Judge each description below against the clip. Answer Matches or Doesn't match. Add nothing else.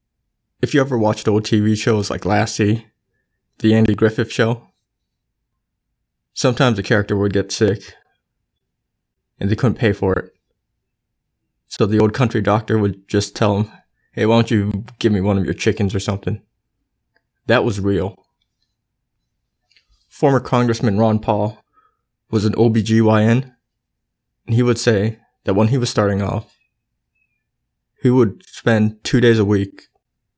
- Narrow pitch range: Matches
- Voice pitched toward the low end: Matches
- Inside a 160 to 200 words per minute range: Doesn't match